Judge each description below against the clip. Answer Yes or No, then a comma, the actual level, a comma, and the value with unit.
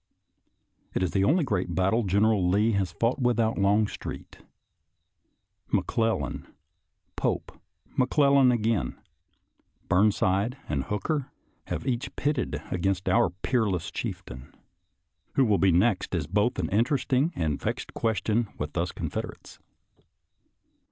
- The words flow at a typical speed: No, slow, 125 wpm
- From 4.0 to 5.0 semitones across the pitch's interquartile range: Yes, average, 4.6 semitones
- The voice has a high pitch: No, low, 105 Hz